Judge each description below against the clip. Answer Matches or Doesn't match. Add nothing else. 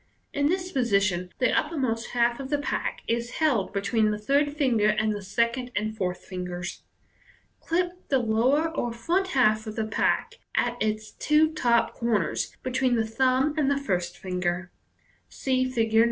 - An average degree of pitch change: Matches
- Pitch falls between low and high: Doesn't match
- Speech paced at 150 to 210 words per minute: Matches